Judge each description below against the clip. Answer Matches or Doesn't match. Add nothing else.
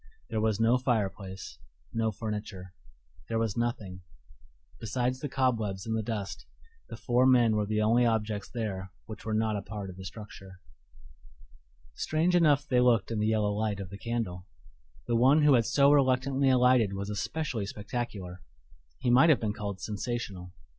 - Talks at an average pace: Matches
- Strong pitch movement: Doesn't match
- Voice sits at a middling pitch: Doesn't match